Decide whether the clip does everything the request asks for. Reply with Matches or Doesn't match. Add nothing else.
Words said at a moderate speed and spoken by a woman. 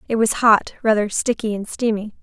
Matches